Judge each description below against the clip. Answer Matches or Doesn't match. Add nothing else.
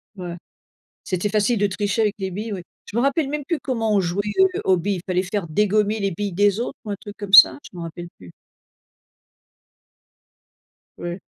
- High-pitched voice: Matches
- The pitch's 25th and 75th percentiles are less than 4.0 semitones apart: Matches